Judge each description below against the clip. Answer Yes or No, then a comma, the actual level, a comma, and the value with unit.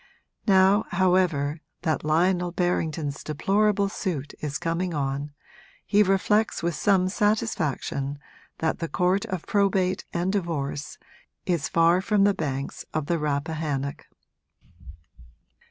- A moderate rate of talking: No, slow, 115 wpm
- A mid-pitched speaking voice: Yes, medium, 175 Hz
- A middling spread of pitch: Yes, average, 4.2 semitones